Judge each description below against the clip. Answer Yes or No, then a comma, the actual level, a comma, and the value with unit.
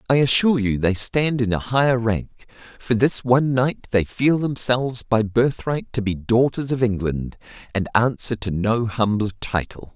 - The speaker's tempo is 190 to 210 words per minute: No, average, 175 wpm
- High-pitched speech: No, low, 115 Hz